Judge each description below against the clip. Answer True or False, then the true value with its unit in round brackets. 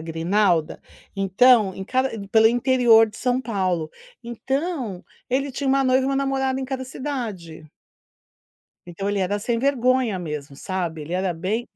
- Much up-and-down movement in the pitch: True (6.0 semitones)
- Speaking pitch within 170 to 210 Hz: False (225 Hz)